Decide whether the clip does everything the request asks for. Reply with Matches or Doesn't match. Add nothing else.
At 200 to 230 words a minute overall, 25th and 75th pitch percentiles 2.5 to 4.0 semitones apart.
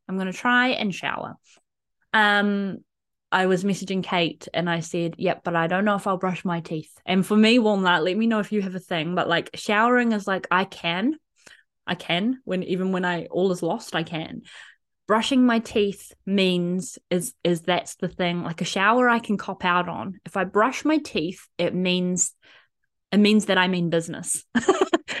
Matches